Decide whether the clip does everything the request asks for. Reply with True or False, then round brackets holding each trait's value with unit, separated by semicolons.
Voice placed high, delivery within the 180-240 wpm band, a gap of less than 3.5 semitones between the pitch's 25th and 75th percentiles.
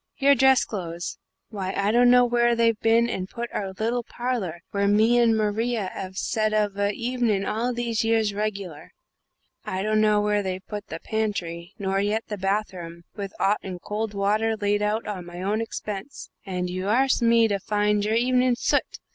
True (210 Hz; 185 wpm; 2.9 semitones)